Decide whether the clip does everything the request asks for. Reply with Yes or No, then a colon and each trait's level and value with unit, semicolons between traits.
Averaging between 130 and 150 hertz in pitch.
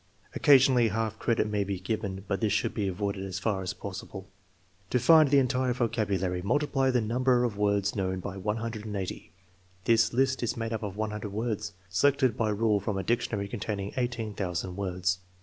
No: low, 105 Hz